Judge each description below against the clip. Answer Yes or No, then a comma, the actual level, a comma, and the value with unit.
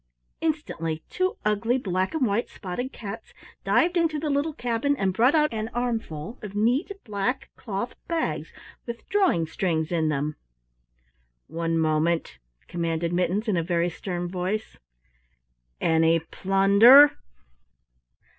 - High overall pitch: Yes, high, 200 Hz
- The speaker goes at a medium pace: No, slow, 125 wpm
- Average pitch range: No, wide, 6.7 semitones